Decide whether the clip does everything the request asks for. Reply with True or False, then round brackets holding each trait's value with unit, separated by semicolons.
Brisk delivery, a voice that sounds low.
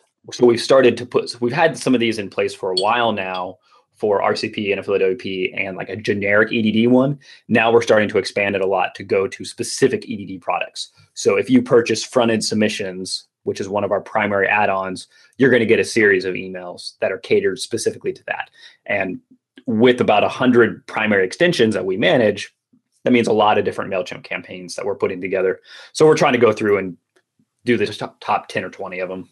True (215 wpm; 120 Hz)